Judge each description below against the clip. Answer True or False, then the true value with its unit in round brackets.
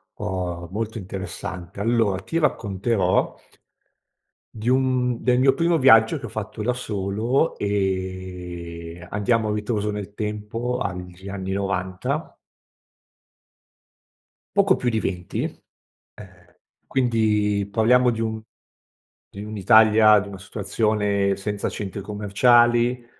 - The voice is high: False (105 Hz)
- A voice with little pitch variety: False (3.5 semitones)